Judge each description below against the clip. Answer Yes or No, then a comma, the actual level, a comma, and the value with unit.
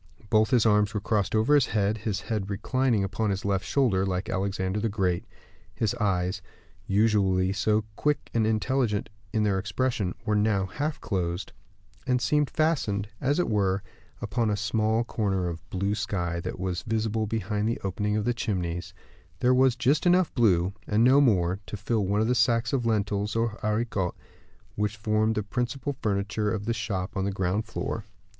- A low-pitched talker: Yes, low, 105 Hz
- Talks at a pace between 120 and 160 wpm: No, average, 180 wpm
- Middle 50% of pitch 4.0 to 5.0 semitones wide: No, average, 2.8 semitones